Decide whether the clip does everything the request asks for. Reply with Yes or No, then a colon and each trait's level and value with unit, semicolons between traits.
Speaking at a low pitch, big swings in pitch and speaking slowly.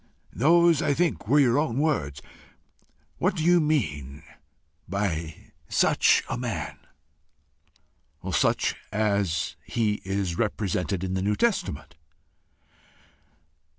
Yes: low, 105 Hz; wide, 8.3 semitones; slow, 105 wpm